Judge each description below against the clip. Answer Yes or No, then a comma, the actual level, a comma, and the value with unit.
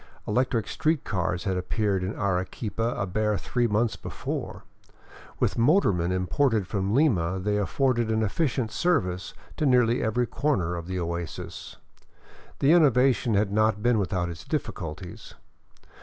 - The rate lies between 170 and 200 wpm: No, average, 140 wpm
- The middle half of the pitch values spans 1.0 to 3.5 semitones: No, average, 4.9 semitones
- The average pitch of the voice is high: No, low, 105 Hz